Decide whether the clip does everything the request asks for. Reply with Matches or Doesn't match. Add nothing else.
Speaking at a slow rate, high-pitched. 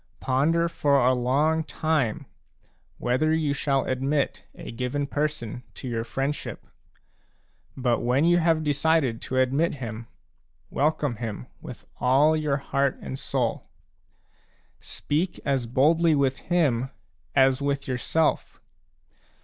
Doesn't match